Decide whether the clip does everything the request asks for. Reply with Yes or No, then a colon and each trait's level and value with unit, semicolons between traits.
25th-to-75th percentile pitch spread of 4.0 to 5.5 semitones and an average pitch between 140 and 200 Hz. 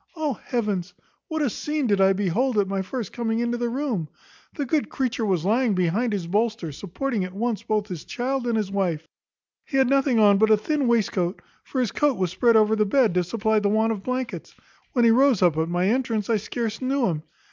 No: average, 4.5 semitones; high, 220 Hz